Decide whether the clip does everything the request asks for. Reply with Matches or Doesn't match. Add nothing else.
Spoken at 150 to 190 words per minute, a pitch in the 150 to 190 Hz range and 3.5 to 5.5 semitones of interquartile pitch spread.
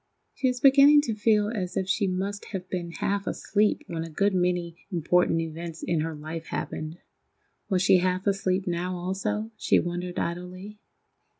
Doesn't match